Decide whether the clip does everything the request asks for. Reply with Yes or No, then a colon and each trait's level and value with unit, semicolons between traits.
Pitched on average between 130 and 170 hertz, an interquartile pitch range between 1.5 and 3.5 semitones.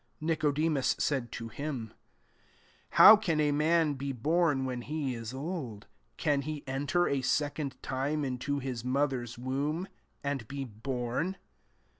Yes: medium, 140 Hz; average, 3.2 semitones